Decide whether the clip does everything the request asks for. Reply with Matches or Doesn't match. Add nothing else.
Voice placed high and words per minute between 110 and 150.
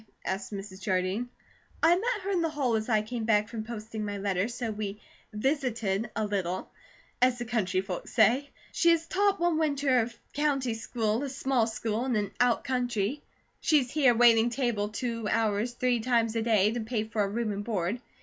Doesn't match